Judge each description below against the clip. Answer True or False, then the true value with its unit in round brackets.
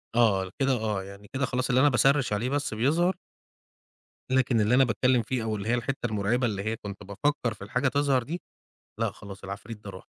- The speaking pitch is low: True (120 Hz)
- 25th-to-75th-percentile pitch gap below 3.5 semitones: False (4.2 semitones)